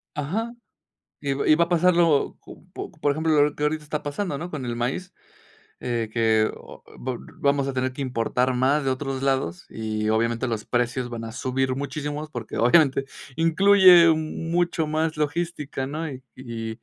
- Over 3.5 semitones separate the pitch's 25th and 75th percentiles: Yes, average, 4.2 semitones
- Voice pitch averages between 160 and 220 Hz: No, medium, 140 Hz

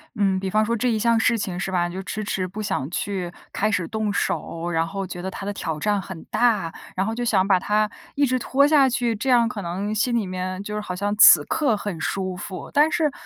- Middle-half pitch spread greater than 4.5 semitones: No, average, 3.7 semitones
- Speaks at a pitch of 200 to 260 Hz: Yes, high, 205 Hz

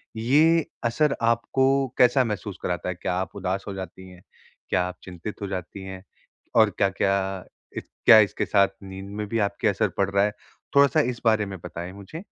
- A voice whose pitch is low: Yes, low, 100 Hz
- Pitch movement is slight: No, average, 3.5 semitones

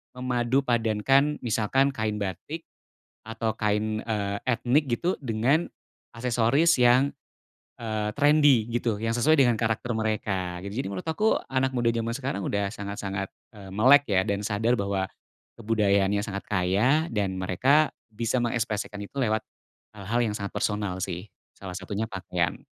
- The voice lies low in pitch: Yes, low, 110 Hz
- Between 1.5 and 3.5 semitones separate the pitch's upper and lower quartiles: No, average, 3.9 semitones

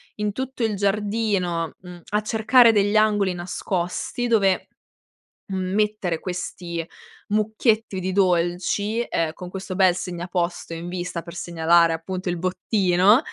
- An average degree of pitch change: Yes, average, 3.1 semitones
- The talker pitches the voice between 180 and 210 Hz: Yes, medium, 185 Hz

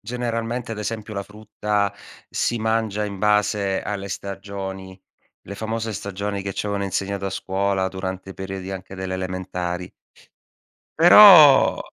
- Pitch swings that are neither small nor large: No, narrow, 2.1 semitones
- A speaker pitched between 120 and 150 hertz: No, low, 100 Hz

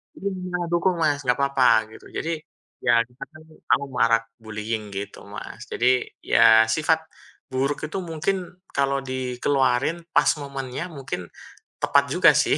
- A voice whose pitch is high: No, low, 135 Hz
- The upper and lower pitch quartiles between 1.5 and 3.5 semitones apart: No, average, 4.8 semitones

